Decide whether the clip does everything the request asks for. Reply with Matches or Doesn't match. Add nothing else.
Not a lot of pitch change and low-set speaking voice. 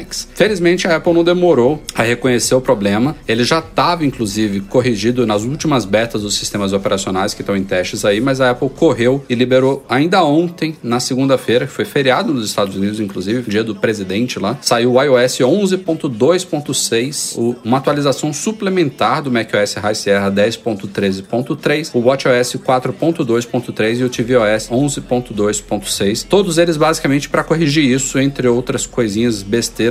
Doesn't match